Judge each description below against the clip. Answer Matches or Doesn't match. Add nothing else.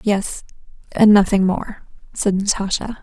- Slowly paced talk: Matches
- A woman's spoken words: Matches